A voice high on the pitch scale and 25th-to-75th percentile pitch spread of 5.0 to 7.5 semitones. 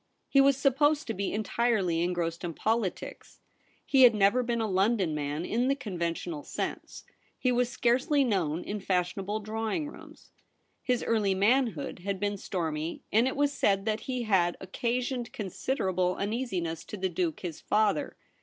Yes: high, 210 Hz; average, 5.3 semitones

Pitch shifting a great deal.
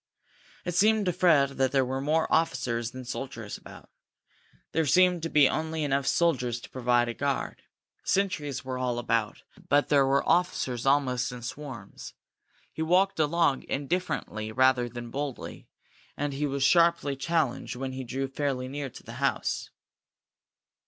No: average, 4.0 semitones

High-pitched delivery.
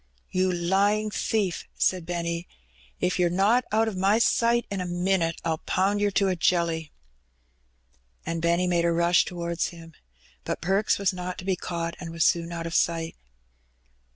No: medium, 180 Hz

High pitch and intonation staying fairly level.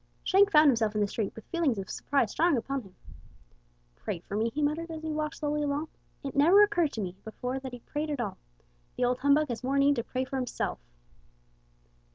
No: very high, 275 Hz; average, 4.7 semitones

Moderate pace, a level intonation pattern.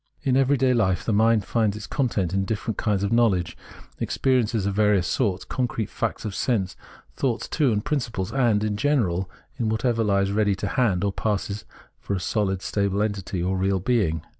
No: average, 190 wpm; average, 3.2 semitones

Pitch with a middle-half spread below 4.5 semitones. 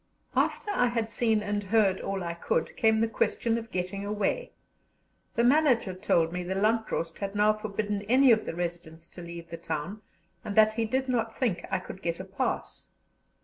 Yes: average, 4.0 semitones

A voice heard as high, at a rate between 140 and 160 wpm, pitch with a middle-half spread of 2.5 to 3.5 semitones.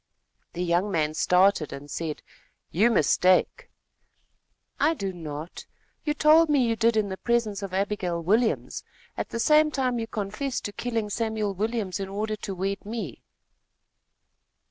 No: high, 205 Hz; average, 150 wpm; average, 4.2 semitones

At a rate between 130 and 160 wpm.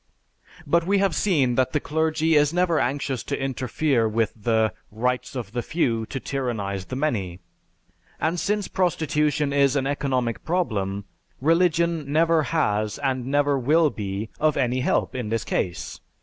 Yes: average, 155 wpm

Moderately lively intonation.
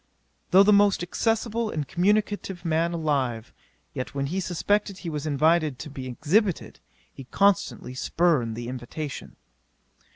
No: wide, 6.2 semitones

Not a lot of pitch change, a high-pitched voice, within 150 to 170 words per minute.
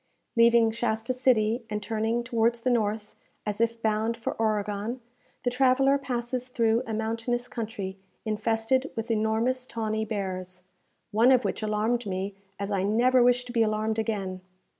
Yes: narrow, 2.2 semitones; high, 225 Hz; average, 155 wpm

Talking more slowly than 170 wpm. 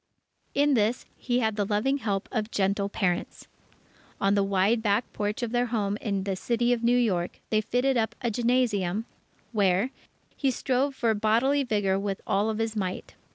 No: average, 175 wpm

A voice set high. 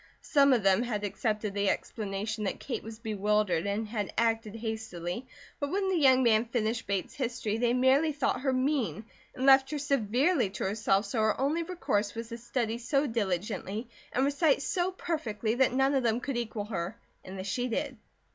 Yes: high, 230 Hz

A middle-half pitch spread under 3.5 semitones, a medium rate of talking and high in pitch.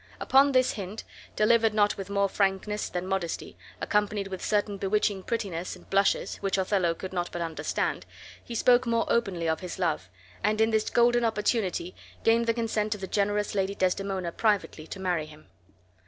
Yes: average, 2.8 semitones; average, 175 wpm; high, 200 Hz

